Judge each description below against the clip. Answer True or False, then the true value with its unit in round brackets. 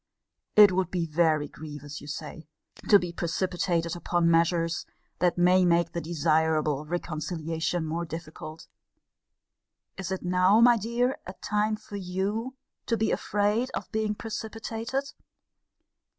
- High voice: False (175 Hz)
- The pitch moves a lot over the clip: False (4.2 semitones)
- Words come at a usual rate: False (130 wpm)